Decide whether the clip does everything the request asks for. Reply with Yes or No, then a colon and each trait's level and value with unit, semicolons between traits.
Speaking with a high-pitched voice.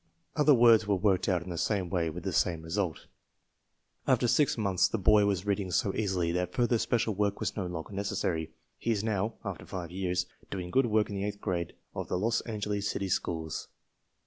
No: low, 100 Hz